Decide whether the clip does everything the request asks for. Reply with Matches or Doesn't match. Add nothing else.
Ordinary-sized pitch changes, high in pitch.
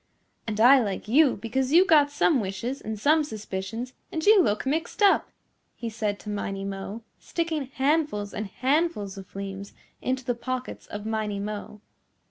Doesn't match